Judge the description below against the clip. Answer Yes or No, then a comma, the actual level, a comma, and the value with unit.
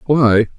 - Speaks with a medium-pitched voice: No, low, 125 Hz